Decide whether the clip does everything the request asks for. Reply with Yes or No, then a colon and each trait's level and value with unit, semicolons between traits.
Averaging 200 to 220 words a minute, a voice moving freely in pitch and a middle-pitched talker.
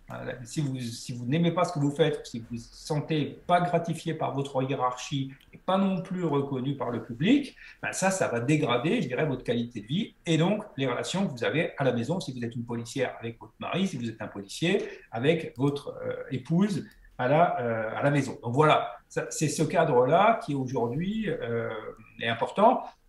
Yes: average, 215 wpm; wide, 5.7 semitones; medium, 145 Hz